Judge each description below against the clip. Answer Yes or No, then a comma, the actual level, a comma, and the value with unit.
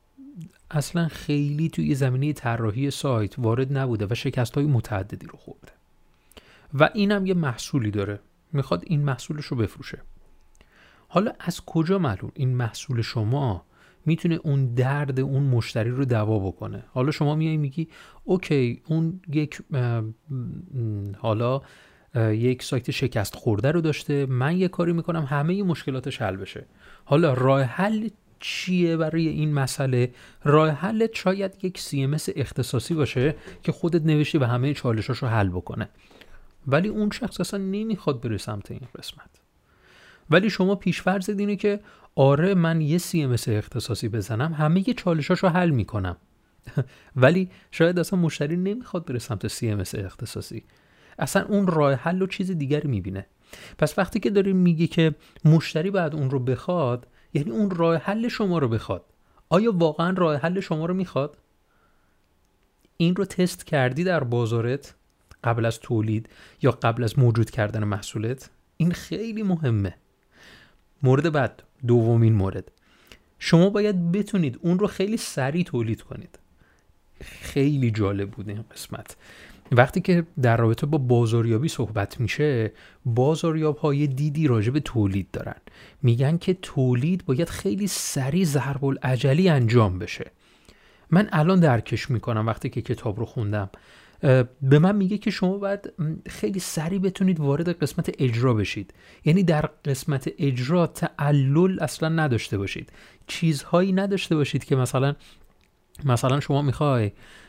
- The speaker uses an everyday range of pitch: No, wide, 6.4 semitones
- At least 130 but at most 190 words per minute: Yes, average, 140 wpm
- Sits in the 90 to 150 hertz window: Yes, medium, 140 Hz